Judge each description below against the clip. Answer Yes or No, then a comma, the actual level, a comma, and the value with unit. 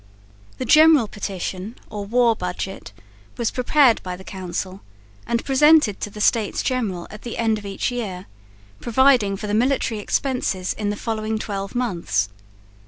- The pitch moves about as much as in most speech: Yes, average, 4.1 semitones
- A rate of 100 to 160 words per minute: Yes, average, 155 wpm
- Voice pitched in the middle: No, high, 215 Hz